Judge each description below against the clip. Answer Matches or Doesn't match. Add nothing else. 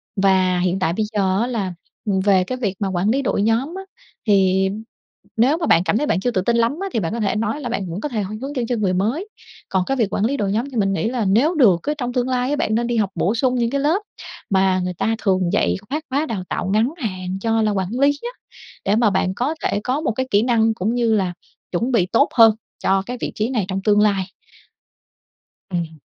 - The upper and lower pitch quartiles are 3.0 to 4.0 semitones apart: Doesn't match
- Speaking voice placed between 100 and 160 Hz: Doesn't match